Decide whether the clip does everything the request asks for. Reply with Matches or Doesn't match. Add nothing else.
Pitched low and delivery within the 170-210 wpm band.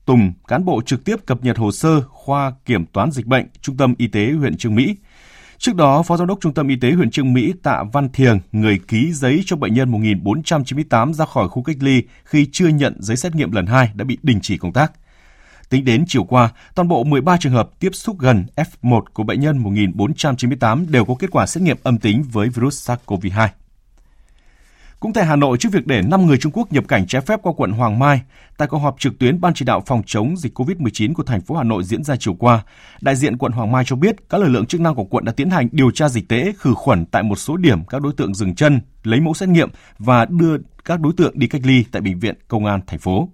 Doesn't match